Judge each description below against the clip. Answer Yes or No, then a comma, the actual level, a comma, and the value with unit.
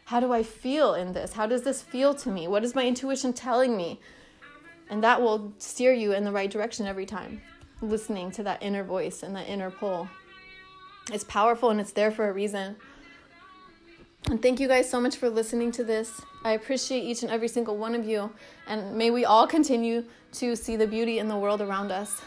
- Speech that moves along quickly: Yes, fast, 215 wpm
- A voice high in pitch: Yes, high, 230 Hz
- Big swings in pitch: No, average, 3.4 semitones